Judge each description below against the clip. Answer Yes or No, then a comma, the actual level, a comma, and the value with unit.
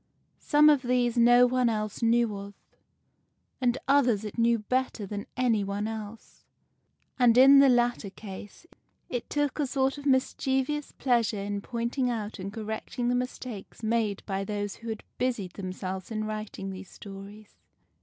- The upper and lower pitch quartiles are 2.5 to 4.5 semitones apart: Yes, average, 3.5 semitones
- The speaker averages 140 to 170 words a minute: Yes, average, 155 wpm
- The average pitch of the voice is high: Yes, high, 230 Hz